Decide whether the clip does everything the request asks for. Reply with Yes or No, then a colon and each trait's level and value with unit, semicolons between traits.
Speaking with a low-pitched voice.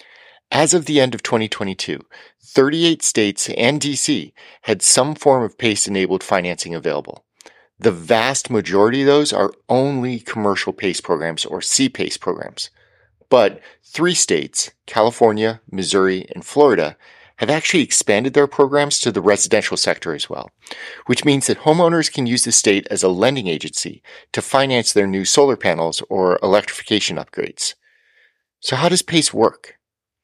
Yes: low, 130 Hz